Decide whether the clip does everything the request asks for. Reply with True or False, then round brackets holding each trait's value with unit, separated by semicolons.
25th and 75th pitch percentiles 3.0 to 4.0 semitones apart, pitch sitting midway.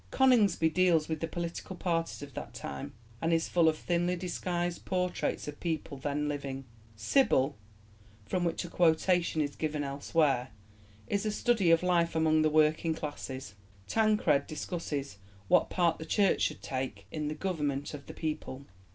True (3.3 semitones; 160 Hz)